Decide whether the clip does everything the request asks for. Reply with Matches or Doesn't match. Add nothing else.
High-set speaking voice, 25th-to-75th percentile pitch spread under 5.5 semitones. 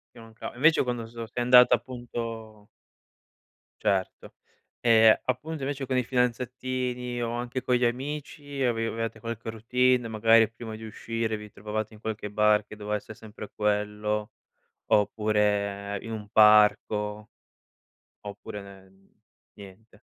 Doesn't match